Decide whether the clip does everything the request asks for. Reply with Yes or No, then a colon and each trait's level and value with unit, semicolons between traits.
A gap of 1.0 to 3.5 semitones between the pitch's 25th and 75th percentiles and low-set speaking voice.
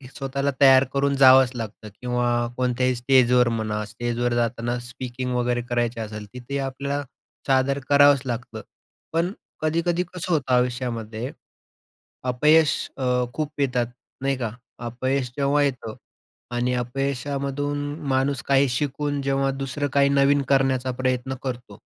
Yes: narrow, 2.4 semitones; low, 130 Hz